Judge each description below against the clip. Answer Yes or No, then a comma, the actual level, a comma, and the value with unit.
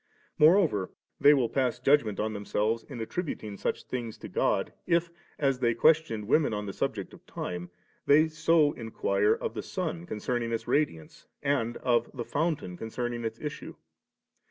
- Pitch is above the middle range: No, low, 120 Hz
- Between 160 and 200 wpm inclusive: Yes, average, 175 wpm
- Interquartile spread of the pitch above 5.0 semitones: Yes, wide, 5.4 semitones